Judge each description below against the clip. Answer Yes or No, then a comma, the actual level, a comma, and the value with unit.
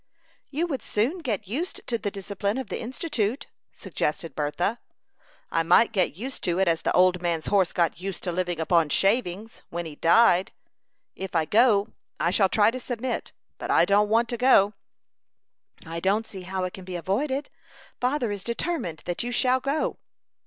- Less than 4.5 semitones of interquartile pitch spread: No, wide, 5.4 semitones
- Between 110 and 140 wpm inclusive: No, average, 180 wpm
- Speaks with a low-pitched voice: No, high, 200 Hz